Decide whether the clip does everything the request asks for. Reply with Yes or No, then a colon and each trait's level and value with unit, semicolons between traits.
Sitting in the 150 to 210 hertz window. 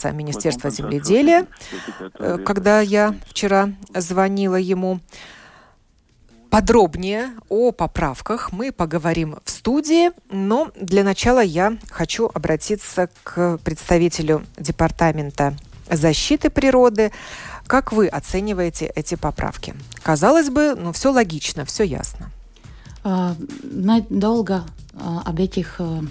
Yes: high, 190 Hz